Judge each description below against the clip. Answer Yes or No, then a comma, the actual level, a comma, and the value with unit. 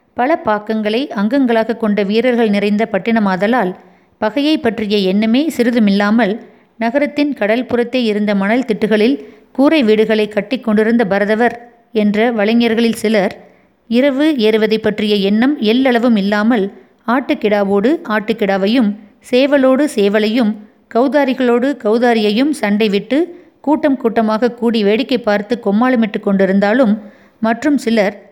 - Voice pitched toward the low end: No, high, 225 Hz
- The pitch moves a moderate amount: Yes, average, 3.0 semitones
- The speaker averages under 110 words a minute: Yes, average, 100 wpm